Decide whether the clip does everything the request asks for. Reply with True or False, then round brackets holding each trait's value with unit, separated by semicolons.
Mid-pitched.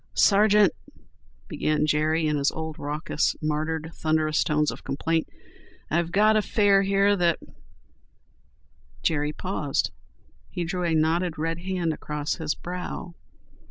True (160 Hz)